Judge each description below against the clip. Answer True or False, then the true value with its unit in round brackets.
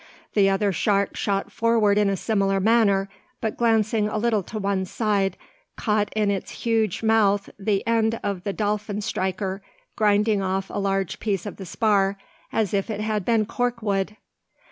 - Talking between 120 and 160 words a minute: False (170 wpm)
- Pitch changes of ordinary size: False (2.0 semitones)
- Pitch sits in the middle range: False (205 Hz)